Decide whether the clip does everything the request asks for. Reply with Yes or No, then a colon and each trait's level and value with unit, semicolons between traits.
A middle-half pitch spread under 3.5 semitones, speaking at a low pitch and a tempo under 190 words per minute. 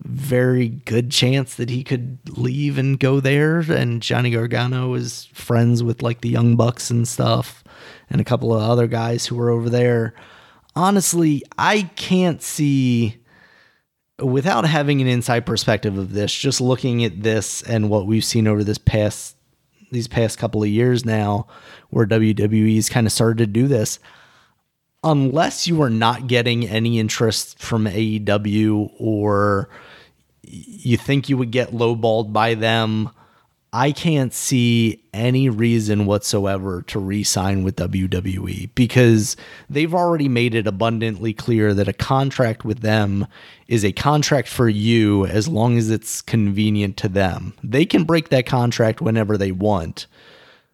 Yes: average, 3.0 semitones; low, 115 Hz; average, 155 wpm